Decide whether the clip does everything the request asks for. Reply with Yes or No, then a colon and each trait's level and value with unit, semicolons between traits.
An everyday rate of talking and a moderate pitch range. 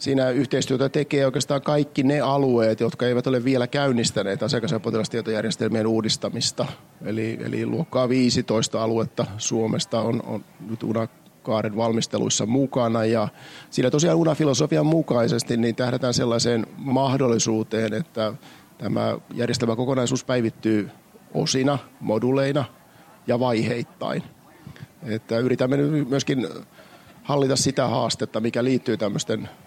Yes: average, 110 wpm; average, 3.2 semitones